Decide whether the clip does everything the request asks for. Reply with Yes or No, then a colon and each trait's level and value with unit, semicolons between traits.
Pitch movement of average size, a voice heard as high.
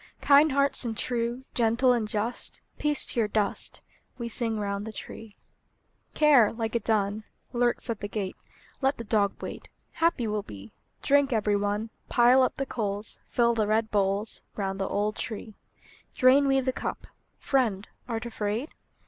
Yes: average, 3.4 semitones; high, 225 Hz